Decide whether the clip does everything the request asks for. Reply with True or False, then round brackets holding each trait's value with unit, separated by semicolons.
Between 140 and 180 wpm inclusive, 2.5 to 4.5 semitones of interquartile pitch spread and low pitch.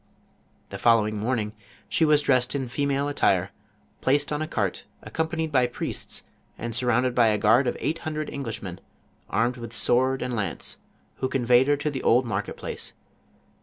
True (165 wpm; 3.9 semitones; 125 Hz)